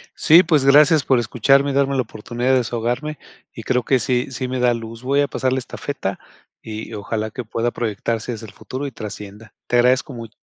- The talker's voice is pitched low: Yes, low, 125 Hz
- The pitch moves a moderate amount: Yes, average, 3.2 semitones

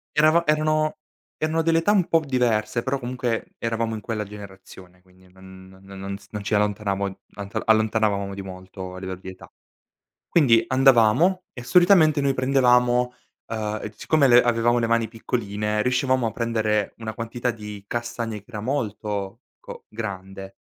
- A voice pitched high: No, low, 115 Hz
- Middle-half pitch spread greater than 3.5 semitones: Yes, average, 4.0 semitones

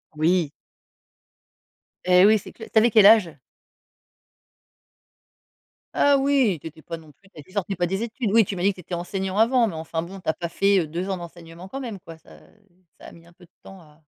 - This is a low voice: No, medium, 185 Hz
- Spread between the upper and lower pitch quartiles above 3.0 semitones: Yes, average, 4.0 semitones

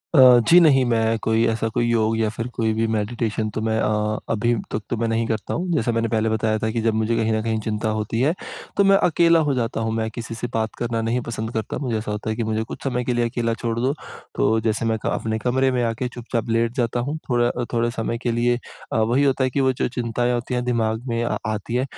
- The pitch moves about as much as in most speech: No, narrow, 1.6 semitones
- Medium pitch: No, low, 115 Hz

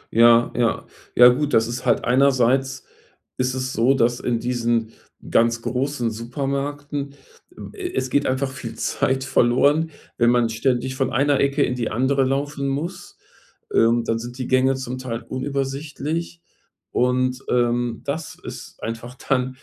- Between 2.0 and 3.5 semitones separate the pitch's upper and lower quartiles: Yes, narrow, 2.5 semitones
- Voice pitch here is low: Yes, low, 130 Hz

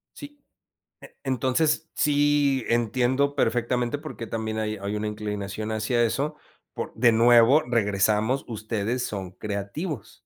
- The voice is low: Yes, low, 120 Hz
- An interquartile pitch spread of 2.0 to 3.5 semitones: No, average, 4.2 semitones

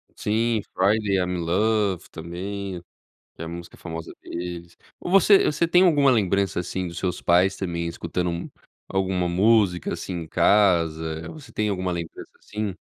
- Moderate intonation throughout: Yes, average, 3.6 semitones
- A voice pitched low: Yes, very low, 95 Hz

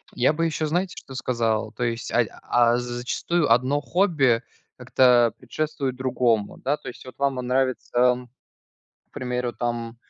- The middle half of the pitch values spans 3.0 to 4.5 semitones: No, narrow, 2.5 semitones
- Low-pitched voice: Yes, low, 125 Hz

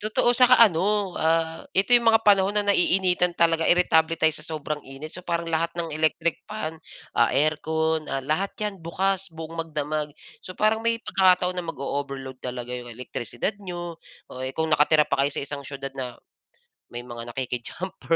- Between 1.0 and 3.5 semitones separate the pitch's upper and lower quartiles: No, average, 4.8 semitones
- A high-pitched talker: No, medium, 160 Hz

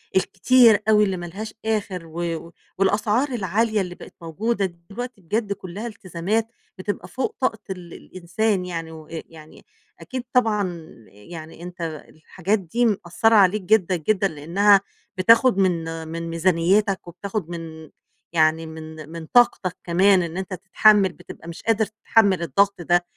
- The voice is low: No, medium, 185 Hz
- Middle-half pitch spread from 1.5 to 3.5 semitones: No, average, 4.1 semitones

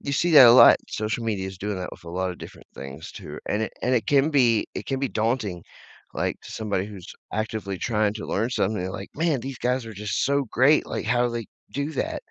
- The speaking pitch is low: Yes, low, 110 Hz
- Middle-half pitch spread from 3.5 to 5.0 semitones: Yes, average, 4.3 semitones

